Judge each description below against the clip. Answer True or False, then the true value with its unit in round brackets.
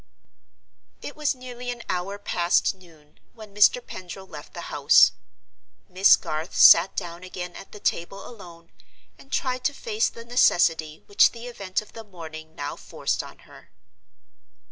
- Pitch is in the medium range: False (195 Hz)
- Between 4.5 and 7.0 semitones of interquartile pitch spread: True (5.6 semitones)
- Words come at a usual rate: True (155 wpm)